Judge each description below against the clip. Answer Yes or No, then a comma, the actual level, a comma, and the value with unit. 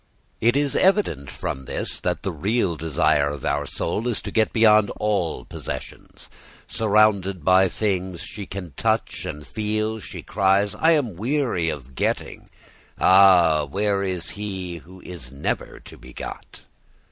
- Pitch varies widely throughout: No, average, 4.8 semitones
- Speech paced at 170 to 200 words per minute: No, average, 155 wpm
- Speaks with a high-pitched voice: No, very low, 95 Hz